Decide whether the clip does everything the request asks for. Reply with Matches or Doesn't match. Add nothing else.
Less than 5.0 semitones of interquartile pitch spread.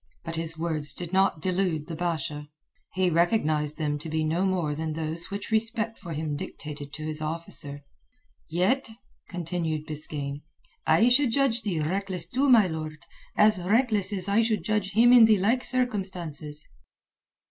Doesn't match